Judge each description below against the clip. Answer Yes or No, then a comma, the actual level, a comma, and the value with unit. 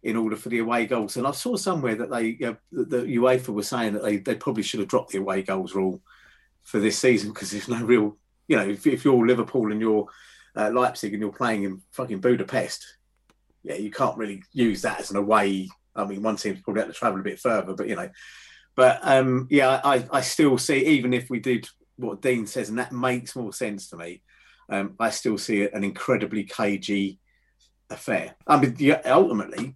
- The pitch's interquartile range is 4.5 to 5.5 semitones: No, average, 3.6 semitones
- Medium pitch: No, low, 110 Hz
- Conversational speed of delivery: No, fast, 220 wpm